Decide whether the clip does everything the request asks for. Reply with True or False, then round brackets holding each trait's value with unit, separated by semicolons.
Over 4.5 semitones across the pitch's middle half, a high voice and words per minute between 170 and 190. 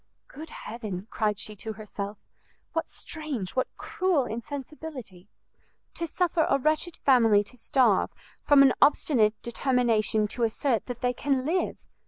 False (5.1 semitones; 250 Hz; 140 wpm)